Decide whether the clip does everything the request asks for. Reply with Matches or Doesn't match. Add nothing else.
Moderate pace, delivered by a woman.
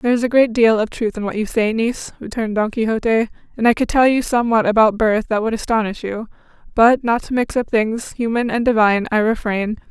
Doesn't match